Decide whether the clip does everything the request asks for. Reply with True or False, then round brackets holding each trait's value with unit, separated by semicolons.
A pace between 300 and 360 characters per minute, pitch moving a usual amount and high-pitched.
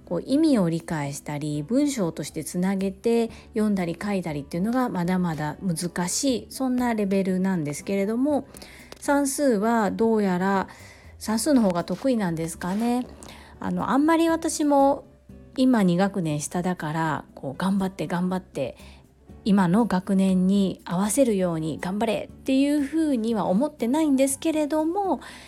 False (310 characters per minute; 6.5 semitones; 195 Hz)